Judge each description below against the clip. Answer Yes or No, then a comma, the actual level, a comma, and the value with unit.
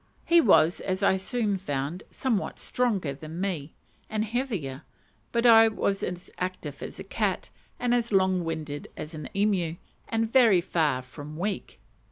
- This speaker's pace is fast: No, average, 160 wpm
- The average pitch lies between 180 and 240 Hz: Yes, high, 190 Hz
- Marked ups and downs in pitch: Yes, wide, 5.8 semitones